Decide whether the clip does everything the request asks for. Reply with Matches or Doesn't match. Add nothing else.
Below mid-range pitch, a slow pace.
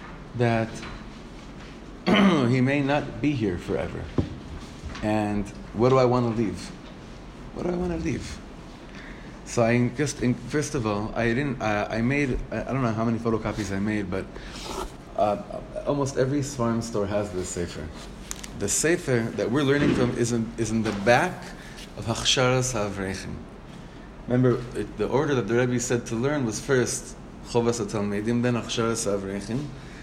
Doesn't match